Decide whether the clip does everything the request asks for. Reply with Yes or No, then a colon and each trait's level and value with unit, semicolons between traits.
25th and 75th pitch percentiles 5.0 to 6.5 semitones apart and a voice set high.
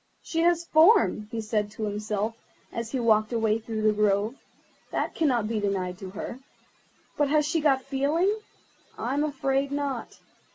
Yes: average, 5.3 semitones; high, 235 Hz